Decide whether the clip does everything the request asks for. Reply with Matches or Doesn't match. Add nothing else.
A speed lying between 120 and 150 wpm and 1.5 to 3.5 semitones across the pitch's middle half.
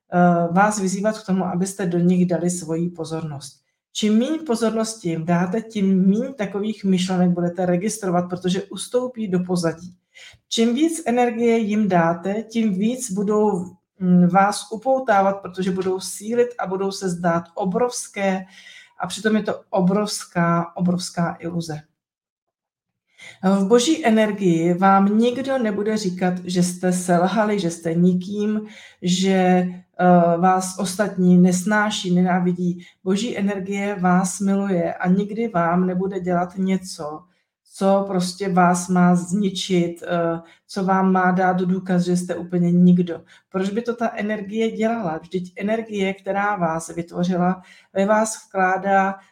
Matches